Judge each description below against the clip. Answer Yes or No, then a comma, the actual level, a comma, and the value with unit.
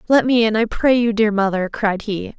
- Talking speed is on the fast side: Yes, fast, 250 wpm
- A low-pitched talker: No, high, 215 Hz